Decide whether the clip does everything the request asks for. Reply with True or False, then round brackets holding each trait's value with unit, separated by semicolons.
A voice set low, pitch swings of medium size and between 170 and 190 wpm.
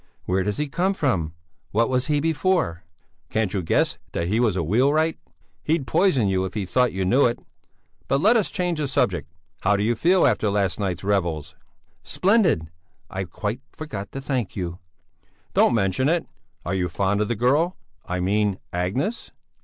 False (110 Hz; 7.6 semitones; 180 wpm)